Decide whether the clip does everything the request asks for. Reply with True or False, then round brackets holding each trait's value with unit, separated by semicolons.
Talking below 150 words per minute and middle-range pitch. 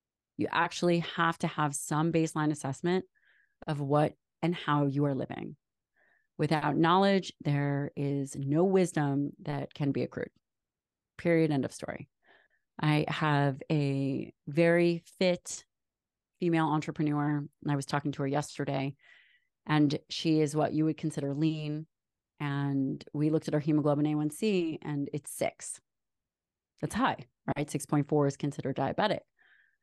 True (135 wpm; 150 Hz)